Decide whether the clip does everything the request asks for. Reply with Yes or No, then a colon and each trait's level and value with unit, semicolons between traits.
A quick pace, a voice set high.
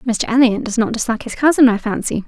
Yes: fast, 235 wpm; high, 235 Hz